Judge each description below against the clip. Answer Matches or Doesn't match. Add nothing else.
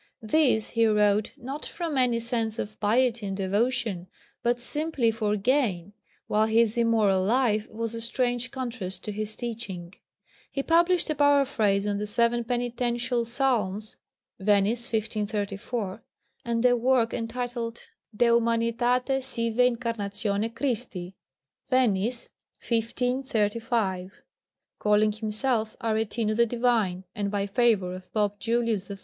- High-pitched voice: Matches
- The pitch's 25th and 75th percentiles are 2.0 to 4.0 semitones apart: Matches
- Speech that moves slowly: Matches